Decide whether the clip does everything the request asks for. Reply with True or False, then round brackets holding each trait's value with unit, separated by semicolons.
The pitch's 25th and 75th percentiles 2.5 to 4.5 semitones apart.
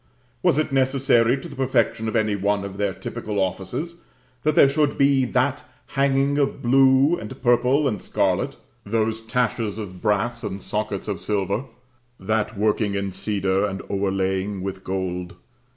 False (5.2 semitones)